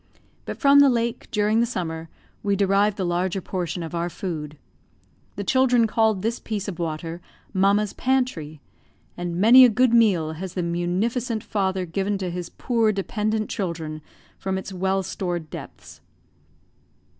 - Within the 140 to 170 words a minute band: Yes, average, 155 wpm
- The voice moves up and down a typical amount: Yes, average, 4.1 semitones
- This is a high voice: Yes, high, 195 Hz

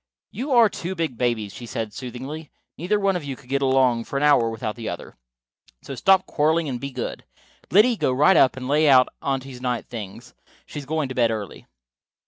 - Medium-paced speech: No, fast, 210 wpm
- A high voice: No, low, 135 Hz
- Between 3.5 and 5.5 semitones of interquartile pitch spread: Yes, average, 4.6 semitones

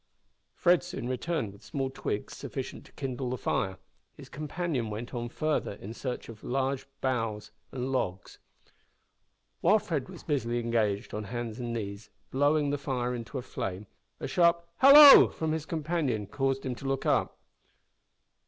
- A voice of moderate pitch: No, low, 130 Hz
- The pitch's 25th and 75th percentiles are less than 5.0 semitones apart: Yes, average, 4.4 semitones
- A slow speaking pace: No, average, 160 wpm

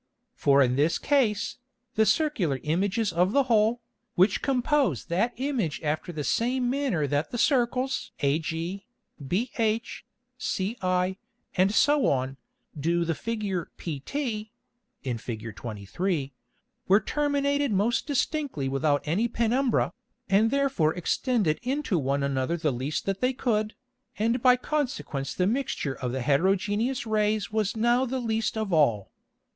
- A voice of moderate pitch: No, high, 210 Hz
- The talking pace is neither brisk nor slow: No, slow, 130 wpm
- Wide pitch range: Yes, wide, 8.1 semitones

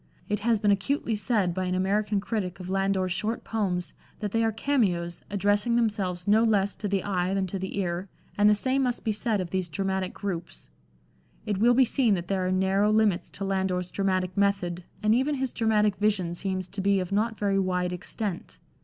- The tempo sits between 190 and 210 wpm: Yes, fast, 205 wpm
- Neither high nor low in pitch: No, high, 200 Hz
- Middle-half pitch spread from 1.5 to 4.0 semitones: Yes, narrow, 2.5 semitones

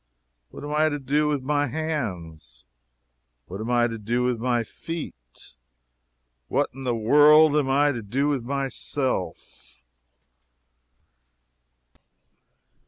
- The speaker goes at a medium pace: No, slow, 120 wpm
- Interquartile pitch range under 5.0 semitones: Yes, average, 4.5 semitones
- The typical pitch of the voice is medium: No, low, 130 Hz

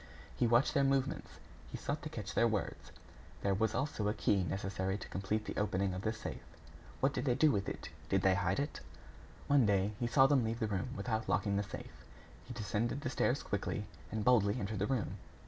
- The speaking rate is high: Yes, fast, 215 wpm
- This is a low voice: Yes, low, 105 Hz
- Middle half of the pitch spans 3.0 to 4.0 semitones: Yes, average, 3.7 semitones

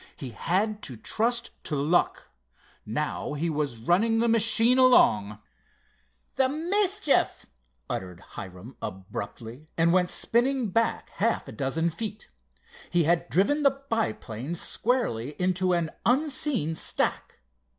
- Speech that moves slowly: Yes, slow, 120 wpm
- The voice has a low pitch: No, medium, 180 Hz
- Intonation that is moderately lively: No, wide, 9.0 semitones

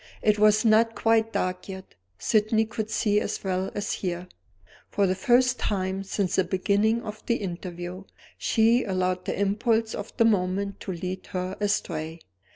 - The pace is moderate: Yes, average, 165 wpm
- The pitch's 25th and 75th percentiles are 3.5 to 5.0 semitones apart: No, average, 3.1 semitones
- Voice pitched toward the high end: Yes, high, 200 Hz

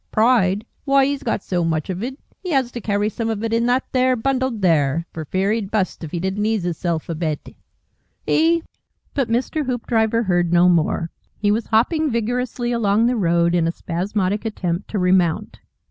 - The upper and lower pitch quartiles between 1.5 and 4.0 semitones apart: No, wide, 5.5 semitones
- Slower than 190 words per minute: No, average, 195 wpm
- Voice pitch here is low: No, high, 210 Hz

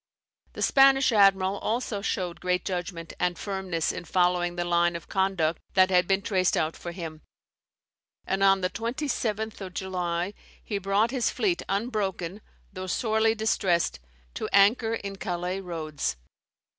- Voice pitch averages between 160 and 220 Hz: Yes, high, 190 Hz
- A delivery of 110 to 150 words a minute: Yes, average, 145 wpm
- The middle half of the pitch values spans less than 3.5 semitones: Yes, average, 3.1 semitones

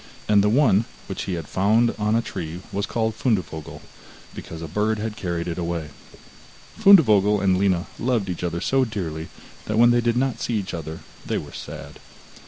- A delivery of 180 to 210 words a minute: Yes, average, 190 wpm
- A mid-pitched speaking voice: No, low, 105 Hz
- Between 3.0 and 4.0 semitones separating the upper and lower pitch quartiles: No, average, 4.9 semitones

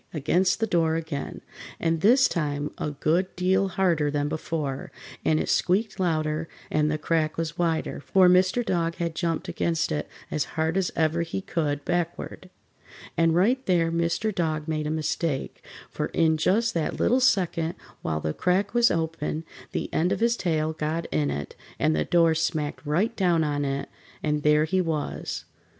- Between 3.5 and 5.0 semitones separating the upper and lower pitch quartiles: No, average, 2.9 semitones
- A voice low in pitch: No, medium, 165 Hz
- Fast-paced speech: No, average, 175 wpm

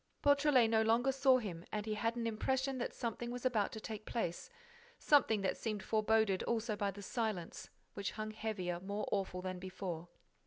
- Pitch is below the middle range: No, high, 220 Hz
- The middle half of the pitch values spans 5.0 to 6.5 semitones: No, average, 3.2 semitones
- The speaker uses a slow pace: No, average, 185 wpm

